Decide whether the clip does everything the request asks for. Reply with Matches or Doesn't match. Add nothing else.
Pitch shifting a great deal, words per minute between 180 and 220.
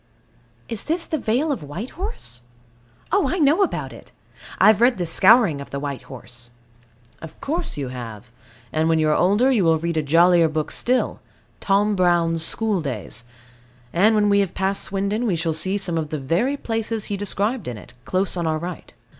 Matches